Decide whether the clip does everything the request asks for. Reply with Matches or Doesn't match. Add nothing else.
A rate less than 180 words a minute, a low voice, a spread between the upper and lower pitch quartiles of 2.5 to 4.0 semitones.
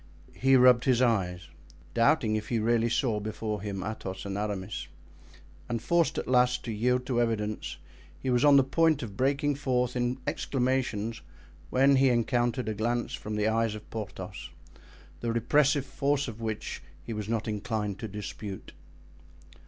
Matches